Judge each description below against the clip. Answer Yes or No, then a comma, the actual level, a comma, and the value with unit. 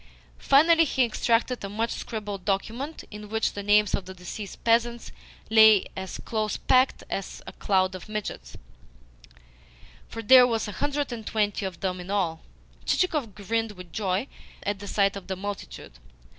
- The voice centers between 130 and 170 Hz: No, high, 210 Hz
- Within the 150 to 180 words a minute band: Yes, average, 165 wpm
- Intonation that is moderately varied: Yes, average, 3.0 semitones